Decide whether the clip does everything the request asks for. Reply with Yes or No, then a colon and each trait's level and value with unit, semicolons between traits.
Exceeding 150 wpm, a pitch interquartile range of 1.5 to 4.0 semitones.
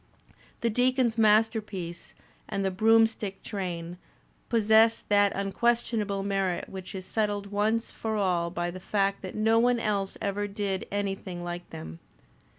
No: average, 140 wpm; average, 2.8 semitones